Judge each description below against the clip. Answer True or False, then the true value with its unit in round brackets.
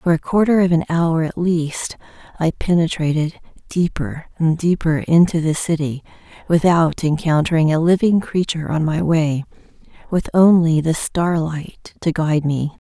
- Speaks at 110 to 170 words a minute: True (140 wpm)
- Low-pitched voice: False (165 Hz)